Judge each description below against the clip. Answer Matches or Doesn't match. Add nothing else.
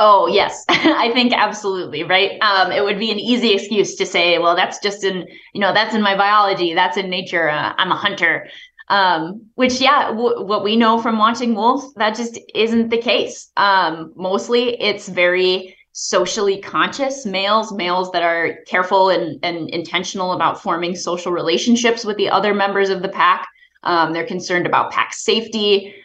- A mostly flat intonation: Doesn't match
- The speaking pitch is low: Doesn't match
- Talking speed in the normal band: Matches